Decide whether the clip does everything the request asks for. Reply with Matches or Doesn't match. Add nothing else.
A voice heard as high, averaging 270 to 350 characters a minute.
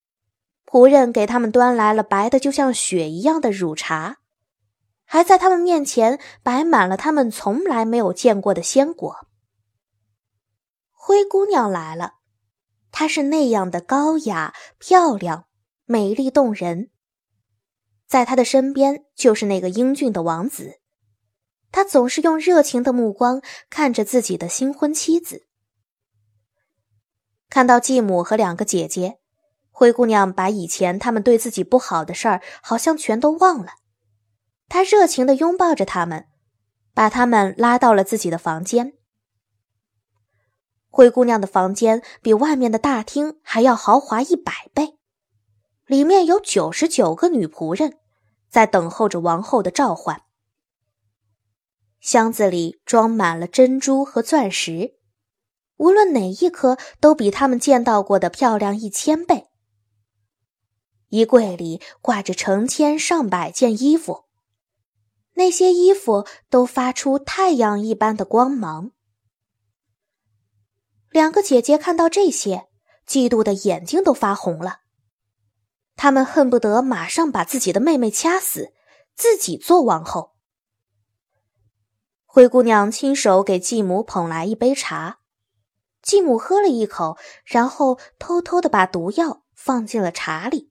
Doesn't match